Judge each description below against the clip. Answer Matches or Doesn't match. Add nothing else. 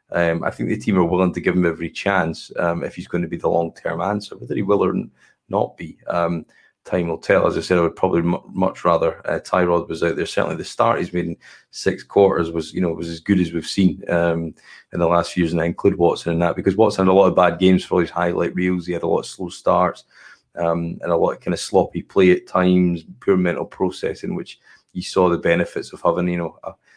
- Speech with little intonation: Matches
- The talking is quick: Matches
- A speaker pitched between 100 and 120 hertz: Doesn't match